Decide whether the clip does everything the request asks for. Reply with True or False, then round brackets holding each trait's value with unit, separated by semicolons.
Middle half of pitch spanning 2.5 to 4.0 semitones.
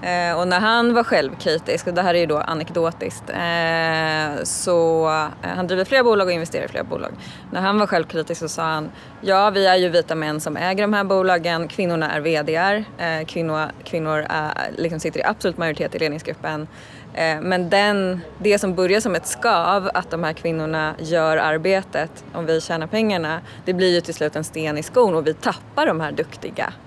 True (2.8 semitones)